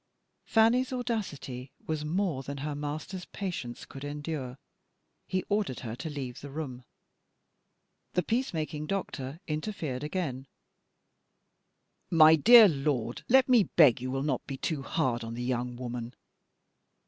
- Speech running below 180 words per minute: Yes, slow, 135 wpm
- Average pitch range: No, wide, 5.8 semitones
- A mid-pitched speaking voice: Yes, medium, 150 Hz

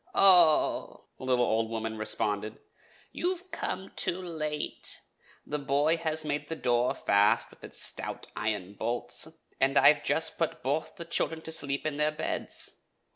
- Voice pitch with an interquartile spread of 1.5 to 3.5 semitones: No, average, 5.2 semitones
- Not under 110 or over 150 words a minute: No, average, 160 wpm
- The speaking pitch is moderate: Yes, medium, 145 Hz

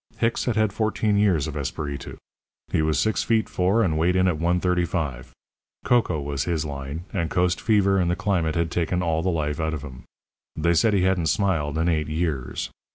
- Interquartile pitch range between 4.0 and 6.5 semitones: No, average, 3.6 semitones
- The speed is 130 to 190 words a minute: No, average, 200 wpm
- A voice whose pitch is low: Yes, very low, 85 Hz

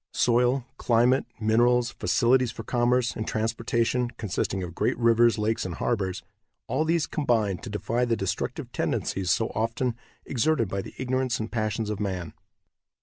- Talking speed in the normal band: Yes, average, 150 wpm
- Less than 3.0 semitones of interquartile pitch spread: Yes, narrow, 2.4 semitones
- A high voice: No, low, 115 Hz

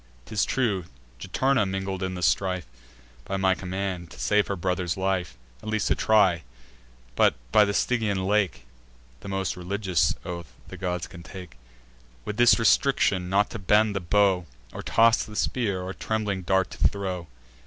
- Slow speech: No, average, 165 wpm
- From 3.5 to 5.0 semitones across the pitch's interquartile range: No, narrow, 2.5 semitones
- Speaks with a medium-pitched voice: No, very low, 95 Hz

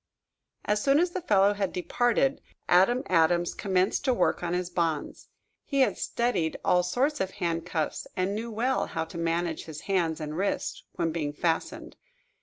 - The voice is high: No, medium, 180 Hz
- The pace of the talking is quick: No, average, 170 wpm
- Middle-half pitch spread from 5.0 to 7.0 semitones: Yes, average, 5.3 semitones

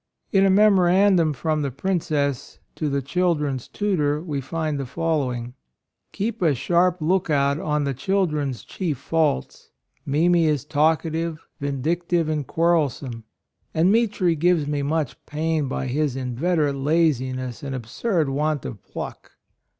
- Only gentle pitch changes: No, average, 3.7 semitones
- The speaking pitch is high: No, medium, 155 Hz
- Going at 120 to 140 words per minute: Yes, slow, 135 wpm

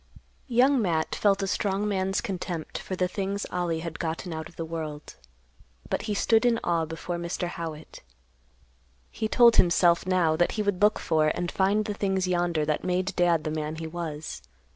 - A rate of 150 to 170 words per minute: No, average, 185 wpm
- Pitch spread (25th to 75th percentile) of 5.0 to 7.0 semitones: No, average, 3.4 semitones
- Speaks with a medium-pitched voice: Yes, medium, 175 Hz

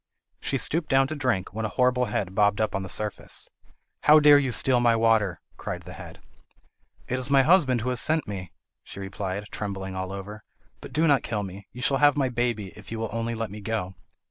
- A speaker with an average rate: No, fast, 220 wpm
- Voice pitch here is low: Yes, low, 115 Hz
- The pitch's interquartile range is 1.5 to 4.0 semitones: No, average, 4.6 semitones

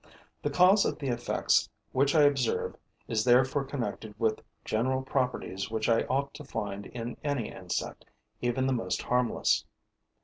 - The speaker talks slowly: No, average, 150 wpm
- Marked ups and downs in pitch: No, average, 3.5 semitones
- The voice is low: Yes, low, 125 Hz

